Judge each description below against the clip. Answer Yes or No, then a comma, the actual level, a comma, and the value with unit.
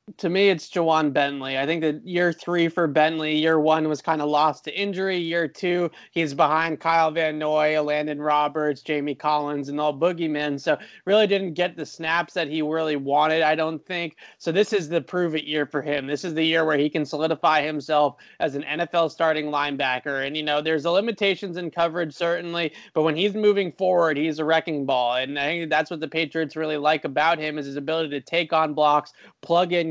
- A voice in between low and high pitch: Yes, medium, 160 Hz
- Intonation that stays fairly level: Yes, narrow, 2.3 semitones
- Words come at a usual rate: No, fast, 215 wpm